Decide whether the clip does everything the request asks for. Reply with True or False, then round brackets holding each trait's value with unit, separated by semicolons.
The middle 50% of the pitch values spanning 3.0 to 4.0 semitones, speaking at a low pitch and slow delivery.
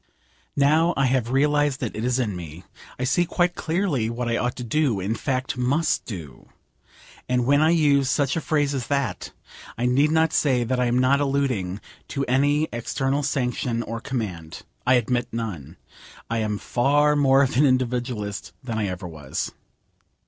False (3.7 semitones; 130 Hz; 180 wpm)